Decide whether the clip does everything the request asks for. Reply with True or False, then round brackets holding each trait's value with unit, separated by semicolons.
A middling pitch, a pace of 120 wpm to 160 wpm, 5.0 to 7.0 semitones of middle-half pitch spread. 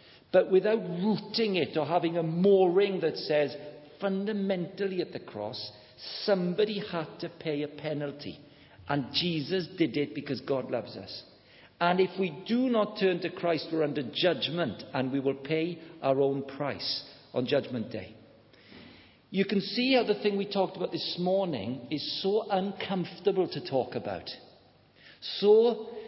True (170 Hz; 155 wpm; 5.4 semitones)